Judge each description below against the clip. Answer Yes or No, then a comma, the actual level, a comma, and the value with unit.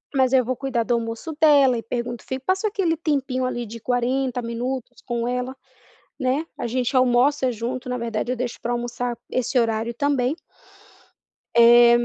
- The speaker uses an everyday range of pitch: No, narrow, 1.9 semitones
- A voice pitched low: No, very high, 250 Hz